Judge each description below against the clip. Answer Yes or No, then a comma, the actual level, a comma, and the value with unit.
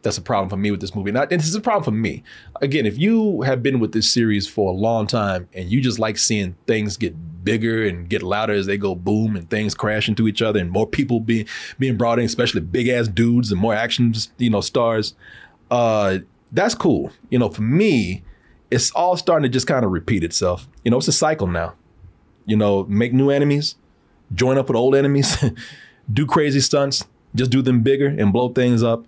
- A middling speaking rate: No, fast, 225 wpm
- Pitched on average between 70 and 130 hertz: Yes, low, 115 Hz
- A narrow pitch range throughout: No, average, 4.2 semitones